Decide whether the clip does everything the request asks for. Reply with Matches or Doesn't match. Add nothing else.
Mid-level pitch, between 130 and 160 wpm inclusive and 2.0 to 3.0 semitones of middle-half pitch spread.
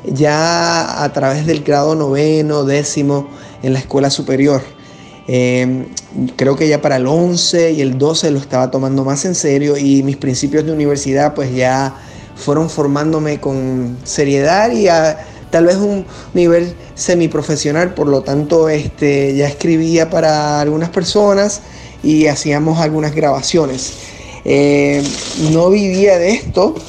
Matches